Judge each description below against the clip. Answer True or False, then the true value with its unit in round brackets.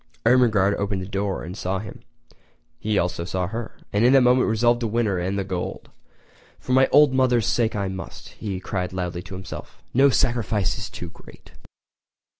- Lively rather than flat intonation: False (4.2 semitones)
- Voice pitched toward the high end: False (105 Hz)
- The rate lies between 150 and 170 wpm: False (185 wpm)